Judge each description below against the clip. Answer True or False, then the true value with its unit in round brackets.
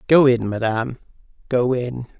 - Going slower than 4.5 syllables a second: True (4.3 syllables/s)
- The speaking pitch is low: True (125 Hz)